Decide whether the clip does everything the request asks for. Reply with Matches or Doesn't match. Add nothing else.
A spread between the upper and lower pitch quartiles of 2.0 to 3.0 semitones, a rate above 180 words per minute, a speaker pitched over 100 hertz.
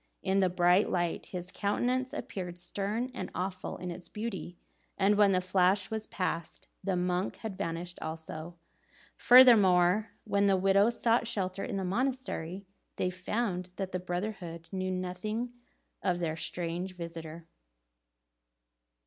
Doesn't match